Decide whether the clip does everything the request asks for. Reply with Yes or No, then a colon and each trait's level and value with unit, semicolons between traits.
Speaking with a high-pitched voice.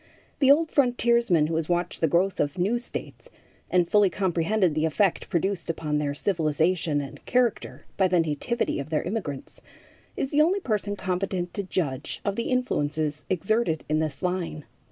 No: medium, 180 Hz